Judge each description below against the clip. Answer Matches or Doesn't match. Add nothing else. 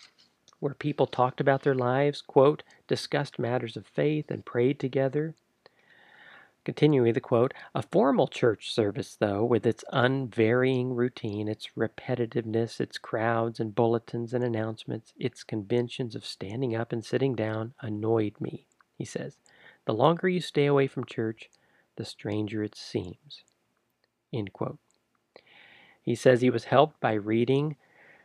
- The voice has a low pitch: Matches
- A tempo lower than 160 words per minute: Matches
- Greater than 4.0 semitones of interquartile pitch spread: Doesn't match